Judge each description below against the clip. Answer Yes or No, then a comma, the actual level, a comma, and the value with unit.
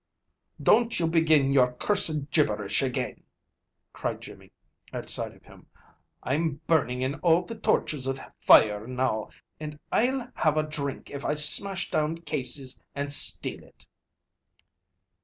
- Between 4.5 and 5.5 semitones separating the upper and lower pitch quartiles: No, average, 3.8 semitones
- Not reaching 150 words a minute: Yes, average, 140 wpm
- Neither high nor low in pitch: Yes, medium, 150 Hz